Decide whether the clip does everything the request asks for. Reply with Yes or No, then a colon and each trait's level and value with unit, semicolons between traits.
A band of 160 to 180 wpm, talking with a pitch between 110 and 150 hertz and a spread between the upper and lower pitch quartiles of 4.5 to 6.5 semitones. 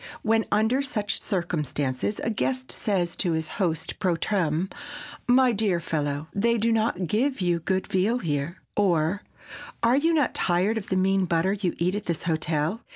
No: average, 170 wpm; high, 190 Hz; average, 4.9 semitones